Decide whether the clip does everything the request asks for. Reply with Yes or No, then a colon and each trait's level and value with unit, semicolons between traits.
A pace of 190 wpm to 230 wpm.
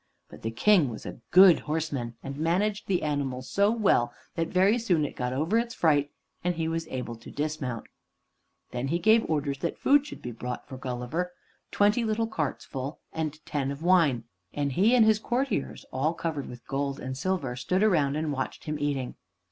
Yes: average, 195 wpm